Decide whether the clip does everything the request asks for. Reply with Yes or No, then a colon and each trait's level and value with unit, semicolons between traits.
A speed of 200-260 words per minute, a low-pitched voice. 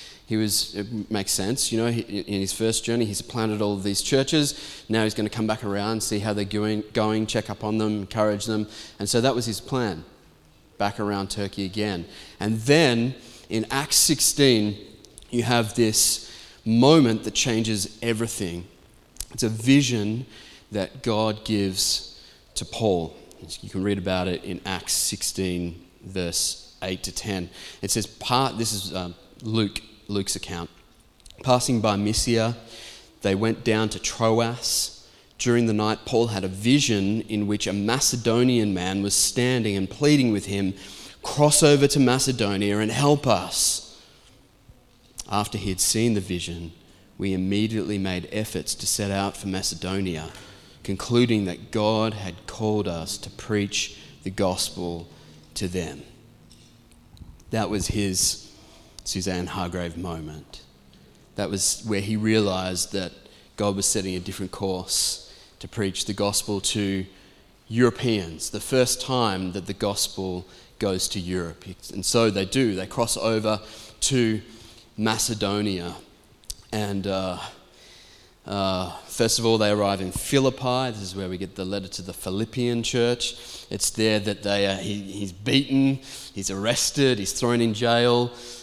No: average, 150 wpm; low, 105 Hz